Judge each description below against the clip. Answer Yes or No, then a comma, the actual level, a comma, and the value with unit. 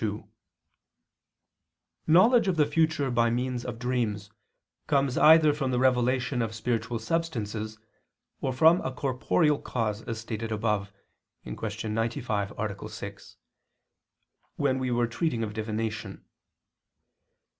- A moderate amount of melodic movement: Yes, average, 3.7 semitones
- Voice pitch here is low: Yes, low, 120 Hz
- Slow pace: Yes, slow, 120 wpm